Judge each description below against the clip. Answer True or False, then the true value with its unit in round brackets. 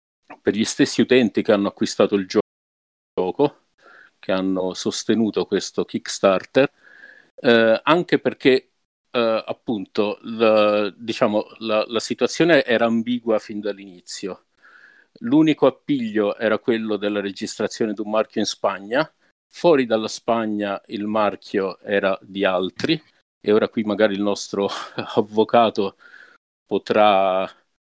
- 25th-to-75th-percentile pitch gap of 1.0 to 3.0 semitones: True (2.6 semitones)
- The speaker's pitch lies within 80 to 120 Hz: True (110 Hz)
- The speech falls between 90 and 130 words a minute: True (120 wpm)